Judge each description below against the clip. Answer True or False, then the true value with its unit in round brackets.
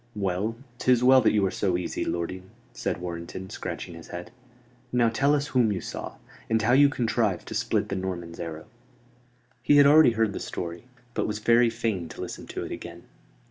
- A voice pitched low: True (105 Hz)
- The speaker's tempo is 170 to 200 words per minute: True (195 wpm)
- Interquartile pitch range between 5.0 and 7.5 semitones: True (5.3 semitones)